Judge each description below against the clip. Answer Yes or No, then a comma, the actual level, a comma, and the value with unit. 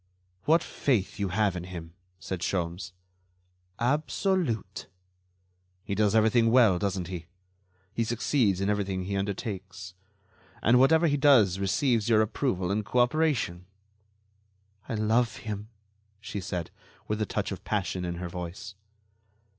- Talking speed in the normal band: No, slow, 130 wpm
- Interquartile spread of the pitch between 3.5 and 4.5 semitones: Yes, average, 4.2 semitones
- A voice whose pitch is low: Yes, low, 105 Hz